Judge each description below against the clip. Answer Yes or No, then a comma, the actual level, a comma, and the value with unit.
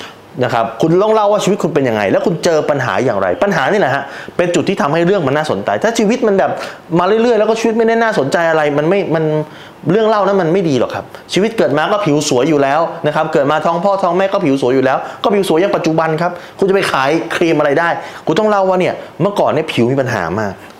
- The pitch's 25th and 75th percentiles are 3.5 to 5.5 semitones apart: Yes, average, 4.6 semitones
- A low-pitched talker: No, medium, 170 Hz